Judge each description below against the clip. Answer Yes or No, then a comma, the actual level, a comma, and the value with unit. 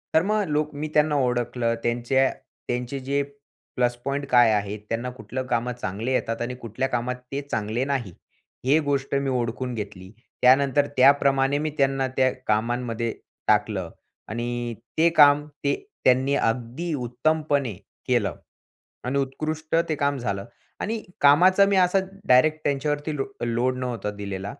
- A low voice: Yes, low, 130 Hz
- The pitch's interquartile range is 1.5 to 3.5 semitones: Yes, average, 3.2 semitones